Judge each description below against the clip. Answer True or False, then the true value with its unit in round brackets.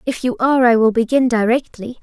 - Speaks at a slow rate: False (205 wpm)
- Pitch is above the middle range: True (245 Hz)